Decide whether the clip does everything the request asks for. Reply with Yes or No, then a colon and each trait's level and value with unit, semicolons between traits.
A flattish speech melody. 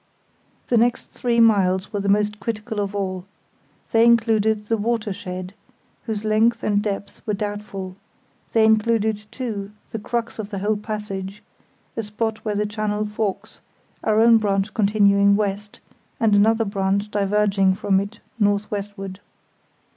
Yes: narrow, 1.7 semitones